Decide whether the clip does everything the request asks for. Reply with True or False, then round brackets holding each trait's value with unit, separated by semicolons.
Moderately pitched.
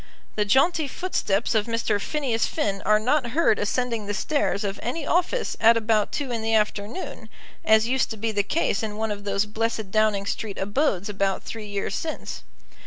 False (220 Hz)